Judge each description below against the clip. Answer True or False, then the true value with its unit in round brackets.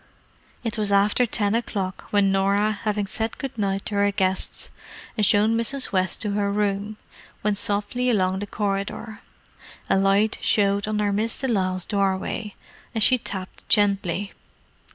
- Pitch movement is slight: True (1.6 semitones)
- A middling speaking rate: True (155 wpm)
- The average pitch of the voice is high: True (205 Hz)